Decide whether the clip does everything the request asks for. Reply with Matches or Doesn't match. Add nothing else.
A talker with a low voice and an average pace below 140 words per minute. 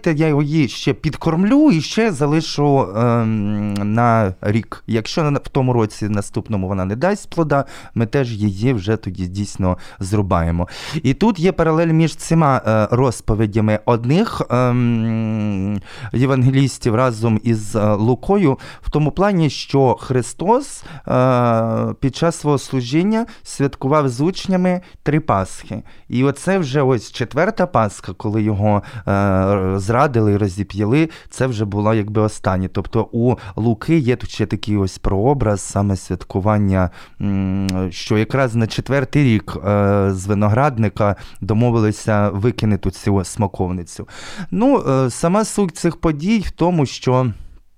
Matches